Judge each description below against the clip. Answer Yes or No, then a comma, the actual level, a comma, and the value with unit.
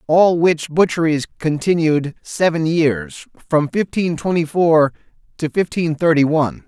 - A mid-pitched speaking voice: Yes, medium, 160 Hz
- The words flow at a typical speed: No, slow, 125 wpm